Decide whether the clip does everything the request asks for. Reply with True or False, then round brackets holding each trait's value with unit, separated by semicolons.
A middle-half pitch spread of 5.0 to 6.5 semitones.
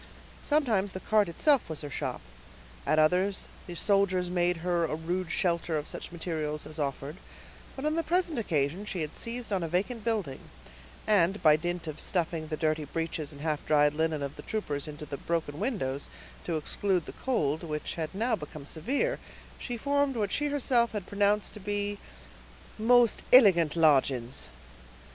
True (5.4 semitones)